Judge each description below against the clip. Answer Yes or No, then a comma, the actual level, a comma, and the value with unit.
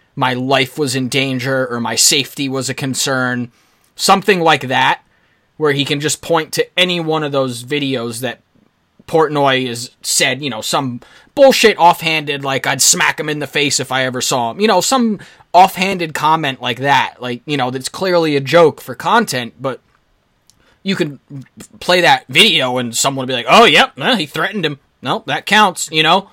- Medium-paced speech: Yes, average, 190 wpm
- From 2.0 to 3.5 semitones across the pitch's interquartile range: No, average, 4.5 semitones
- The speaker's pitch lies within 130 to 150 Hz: Yes, medium, 140 Hz